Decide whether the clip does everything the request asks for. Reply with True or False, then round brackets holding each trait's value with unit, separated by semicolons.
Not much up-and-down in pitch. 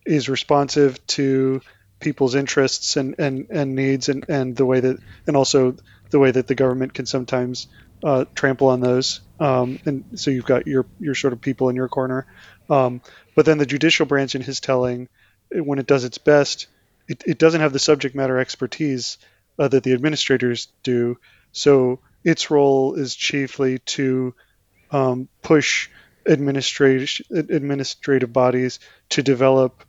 True (1.8 semitones)